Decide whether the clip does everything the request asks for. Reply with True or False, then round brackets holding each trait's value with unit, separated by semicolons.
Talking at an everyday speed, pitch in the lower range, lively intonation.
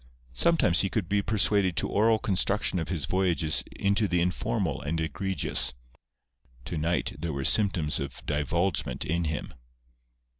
False (145 wpm; 85 Hz; 4.2 semitones)